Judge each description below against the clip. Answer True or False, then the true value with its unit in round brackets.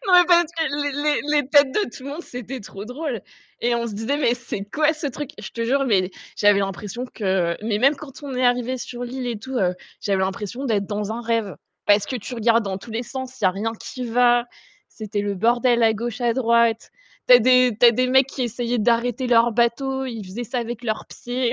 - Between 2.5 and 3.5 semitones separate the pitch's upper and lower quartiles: True (2.9 semitones)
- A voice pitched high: True (240 Hz)